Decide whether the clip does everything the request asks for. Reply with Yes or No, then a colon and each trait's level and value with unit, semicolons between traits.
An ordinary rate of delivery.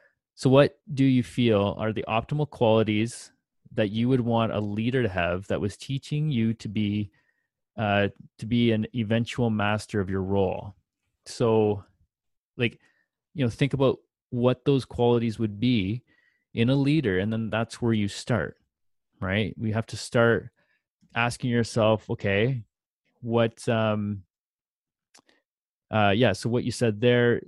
Yes: average, 150 wpm